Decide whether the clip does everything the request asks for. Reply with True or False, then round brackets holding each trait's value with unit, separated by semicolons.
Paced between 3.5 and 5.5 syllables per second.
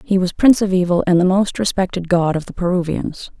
False (5.9 syllables/s)